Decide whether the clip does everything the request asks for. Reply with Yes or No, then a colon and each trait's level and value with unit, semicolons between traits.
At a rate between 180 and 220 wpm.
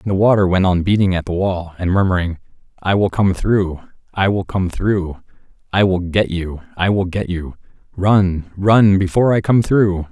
Yes: average, 185 wpm